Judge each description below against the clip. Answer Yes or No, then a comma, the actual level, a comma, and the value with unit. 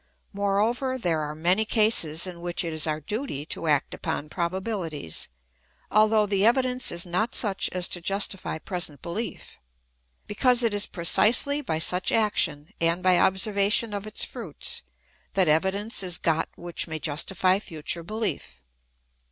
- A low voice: No, medium, 185 Hz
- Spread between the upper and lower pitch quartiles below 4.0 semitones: No, average, 4.4 semitones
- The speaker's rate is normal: Yes, average, 150 wpm